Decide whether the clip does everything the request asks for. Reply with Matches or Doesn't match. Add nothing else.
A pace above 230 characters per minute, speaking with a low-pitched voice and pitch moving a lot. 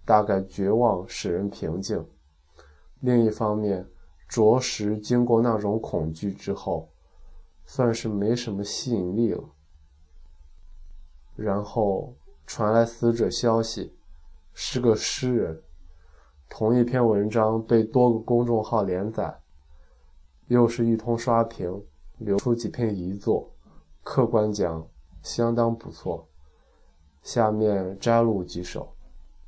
Doesn't match